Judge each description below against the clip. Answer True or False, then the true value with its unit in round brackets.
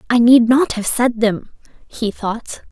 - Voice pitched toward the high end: True (235 Hz)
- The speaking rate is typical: True (175 wpm)